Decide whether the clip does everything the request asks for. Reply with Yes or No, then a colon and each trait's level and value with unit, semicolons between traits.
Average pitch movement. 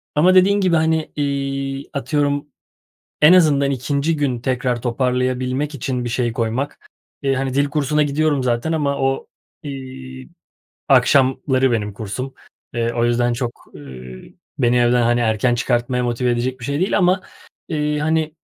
Yes: average, 3.2 semitones